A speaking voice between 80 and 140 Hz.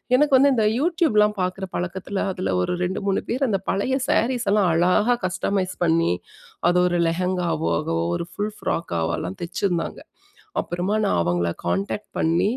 No: medium, 185 Hz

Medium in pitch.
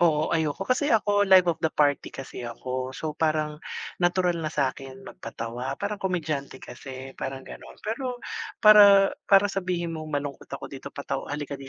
Yes: medium, 155 Hz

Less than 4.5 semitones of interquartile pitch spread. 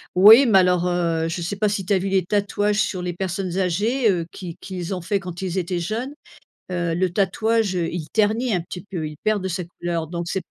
Yes: average, 2.8 semitones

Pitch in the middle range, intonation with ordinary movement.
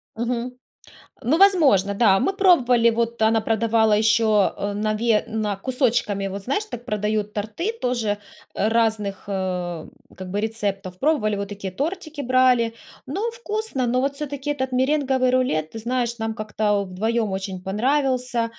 No: high, 230 Hz; average, 3.9 semitones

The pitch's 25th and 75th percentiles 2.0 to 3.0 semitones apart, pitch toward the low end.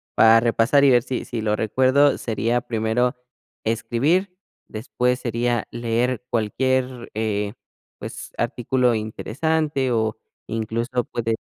Yes: narrow, 2.4 semitones; low, 120 Hz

